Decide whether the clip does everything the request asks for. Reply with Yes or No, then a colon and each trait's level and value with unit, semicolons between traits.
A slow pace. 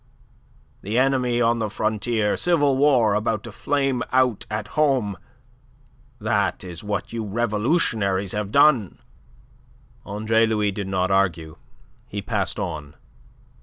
Yes: slow, 125 wpm